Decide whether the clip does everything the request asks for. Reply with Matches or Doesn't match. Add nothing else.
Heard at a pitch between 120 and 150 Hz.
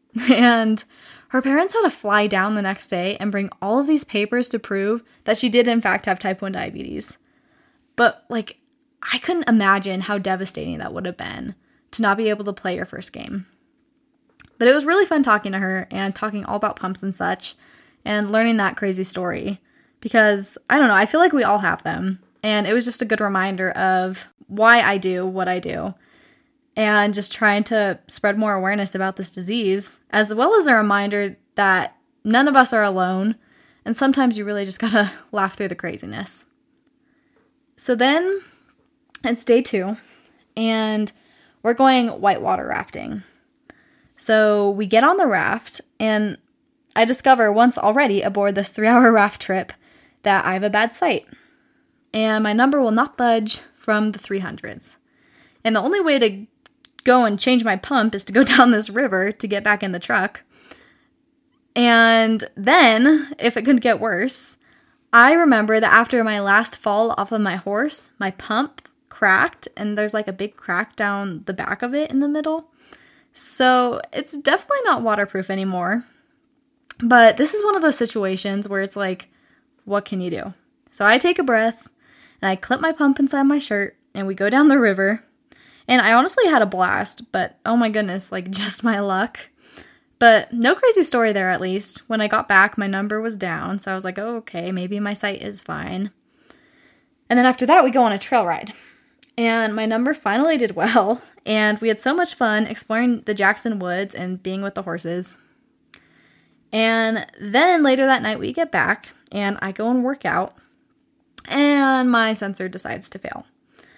Doesn't match